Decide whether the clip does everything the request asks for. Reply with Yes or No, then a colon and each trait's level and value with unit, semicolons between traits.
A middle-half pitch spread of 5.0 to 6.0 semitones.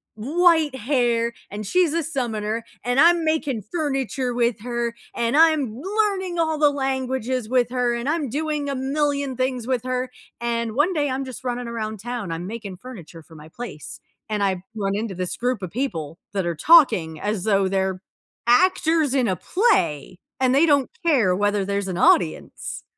Yes: wide, 5.5 semitones